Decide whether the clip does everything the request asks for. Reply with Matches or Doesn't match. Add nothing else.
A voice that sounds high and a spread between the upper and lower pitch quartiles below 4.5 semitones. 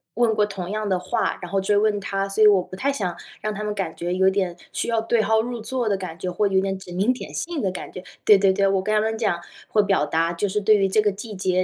Matches